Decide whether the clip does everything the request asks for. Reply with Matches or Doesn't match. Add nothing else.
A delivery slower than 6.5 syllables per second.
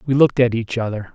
Doesn't match